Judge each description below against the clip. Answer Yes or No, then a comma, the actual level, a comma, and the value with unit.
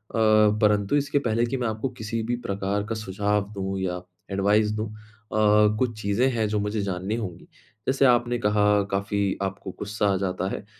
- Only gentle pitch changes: Yes, narrow, 2.2 semitones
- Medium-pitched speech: No, low, 105 Hz